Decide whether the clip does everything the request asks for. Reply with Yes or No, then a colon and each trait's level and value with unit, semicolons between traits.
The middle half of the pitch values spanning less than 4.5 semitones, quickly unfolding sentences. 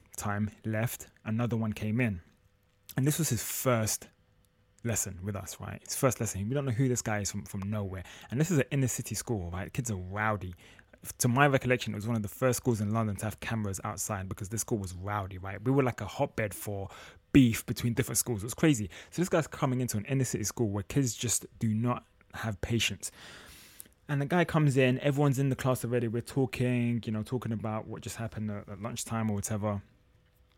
Yes: average, 3.5 semitones; fast, 225 wpm